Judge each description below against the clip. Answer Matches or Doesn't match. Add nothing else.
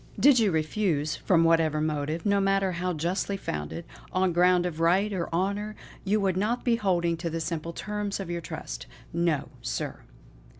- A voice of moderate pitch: Matches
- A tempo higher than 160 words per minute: Matches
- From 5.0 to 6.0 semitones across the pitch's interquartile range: Doesn't match